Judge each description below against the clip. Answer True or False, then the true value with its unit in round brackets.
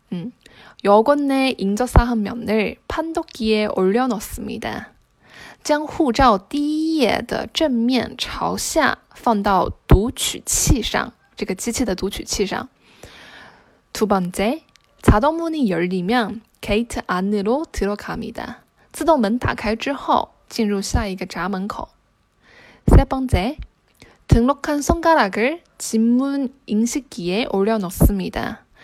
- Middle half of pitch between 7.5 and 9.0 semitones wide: False (5.4 semitones)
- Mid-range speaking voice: False (235 Hz)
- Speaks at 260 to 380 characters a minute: False (215 characters per minute)